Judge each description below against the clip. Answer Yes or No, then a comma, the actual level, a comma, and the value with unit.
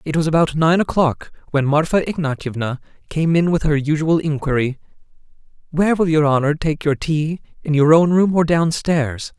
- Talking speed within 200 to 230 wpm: No, average, 175 wpm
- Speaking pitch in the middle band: Yes, medium, 155 Hz